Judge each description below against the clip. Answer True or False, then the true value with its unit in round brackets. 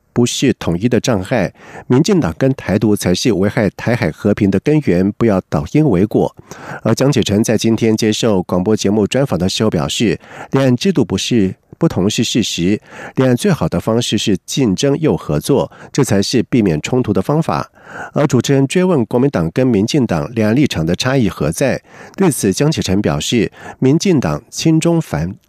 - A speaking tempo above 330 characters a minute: False (280 characters per minute)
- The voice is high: False (120 Hz)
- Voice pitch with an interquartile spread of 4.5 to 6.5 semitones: True (5.2 semitones)